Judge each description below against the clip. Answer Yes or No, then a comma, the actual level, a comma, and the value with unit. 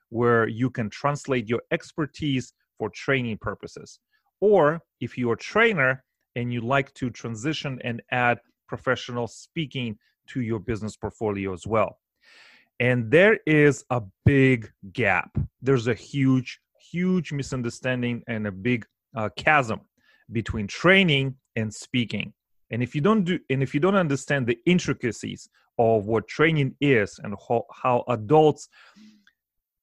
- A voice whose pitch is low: Yes, low, 125 Hz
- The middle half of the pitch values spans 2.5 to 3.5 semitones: No, average, 3.9 semitones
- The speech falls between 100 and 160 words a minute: Yes, average, 140 wpm